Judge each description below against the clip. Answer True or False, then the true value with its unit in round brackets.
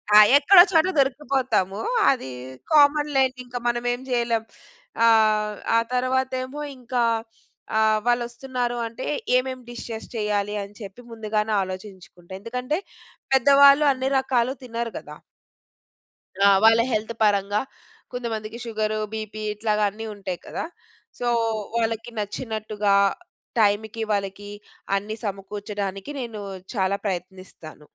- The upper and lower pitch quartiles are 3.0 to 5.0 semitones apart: True (3.5 semitones)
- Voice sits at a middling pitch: False (225 Hz)